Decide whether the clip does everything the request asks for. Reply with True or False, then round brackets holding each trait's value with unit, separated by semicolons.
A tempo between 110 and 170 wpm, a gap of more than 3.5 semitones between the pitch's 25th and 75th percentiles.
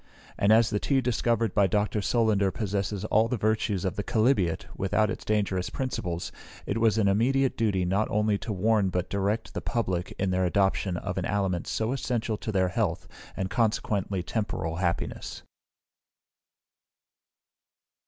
False (155 wpm; 2.8 semitones)